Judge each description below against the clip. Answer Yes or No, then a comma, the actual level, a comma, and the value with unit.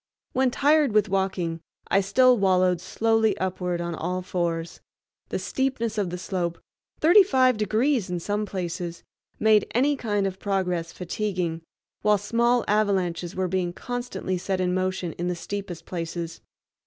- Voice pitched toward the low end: No, high, 190 Hz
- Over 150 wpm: No, average, 140 wpm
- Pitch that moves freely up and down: No, average, 3.6 semitones